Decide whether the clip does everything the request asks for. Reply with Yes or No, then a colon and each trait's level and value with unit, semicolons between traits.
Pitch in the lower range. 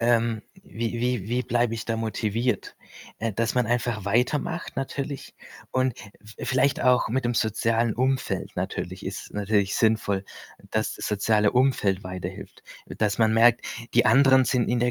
Yes: low, 115 Hz